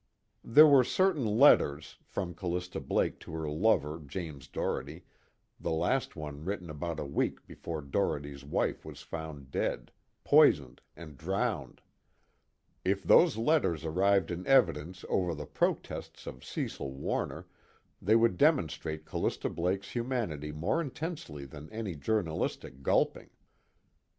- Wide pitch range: Yes, wide, 6.4 semitones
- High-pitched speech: No, very low, 85 Hz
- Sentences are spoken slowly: Yes, slow, 130 wpm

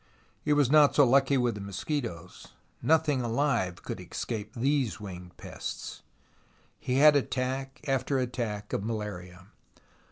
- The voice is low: Yes, low, 125 Hz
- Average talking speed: No, slow, 130 wpm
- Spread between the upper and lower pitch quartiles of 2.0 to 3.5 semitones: No, average, 5.2 semitones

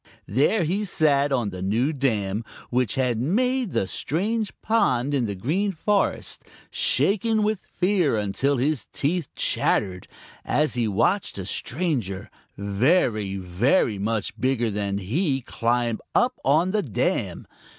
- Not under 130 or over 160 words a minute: Yes, slow, 135 wpm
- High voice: No, low, 135 Hz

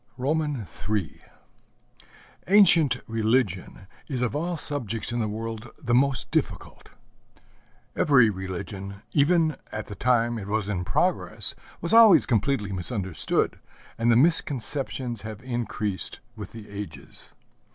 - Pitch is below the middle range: Yes, low, 115 Hz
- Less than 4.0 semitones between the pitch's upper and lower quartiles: No, average, 5.1 semitones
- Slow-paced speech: Yes, slow, 120 wpm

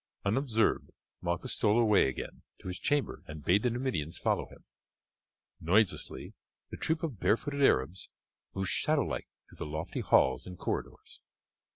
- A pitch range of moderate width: No, wide, 6.7 semitones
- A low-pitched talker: Yes, low, 100 Hz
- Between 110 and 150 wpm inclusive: Yes, average, 145 wpm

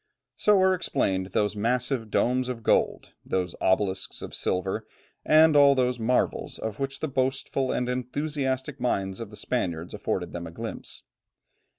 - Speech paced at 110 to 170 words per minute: Yes, average, 155 wpm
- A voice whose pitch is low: Yes, low, 125 Hz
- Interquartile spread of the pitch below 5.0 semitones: No, average, 5.3 semitones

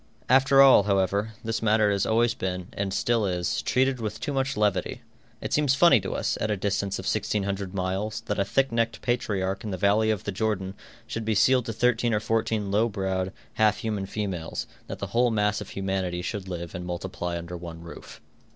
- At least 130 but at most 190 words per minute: No, fast, 205 wpm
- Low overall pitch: Yes, low, 105 Hz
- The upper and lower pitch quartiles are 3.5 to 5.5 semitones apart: No, average, 3.0 semitones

